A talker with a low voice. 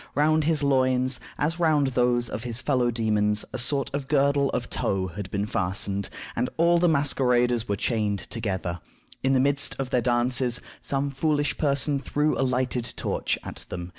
Yes: low, 130 Hz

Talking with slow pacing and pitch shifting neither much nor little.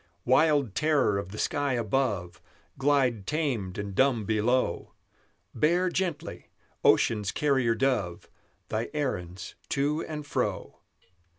No: slow, 110 wpm; wide, 6.0 semitones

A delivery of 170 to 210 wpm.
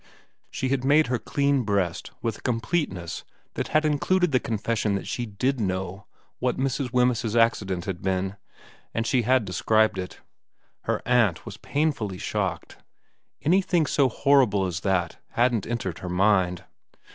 No: average, 155 wpm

